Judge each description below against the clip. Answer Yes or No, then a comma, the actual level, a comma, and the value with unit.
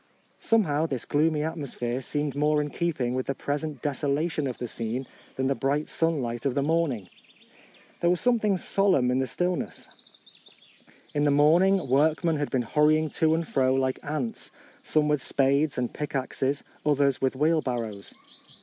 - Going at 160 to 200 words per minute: Yes, average, 170 wpm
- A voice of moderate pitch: Yes, medium, 145 Hz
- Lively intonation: No, average, 3.3 semitones